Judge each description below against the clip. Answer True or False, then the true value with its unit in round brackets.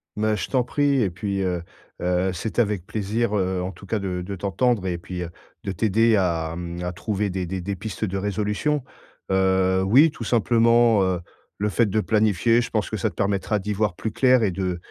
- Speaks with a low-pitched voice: True (100 Hz)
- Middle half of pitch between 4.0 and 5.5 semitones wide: False (3.2 semitones)